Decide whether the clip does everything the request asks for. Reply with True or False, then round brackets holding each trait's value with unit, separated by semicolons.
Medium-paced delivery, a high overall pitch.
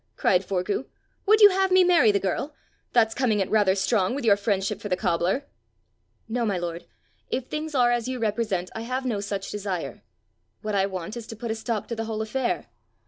False (210 wpm; 220 Hz)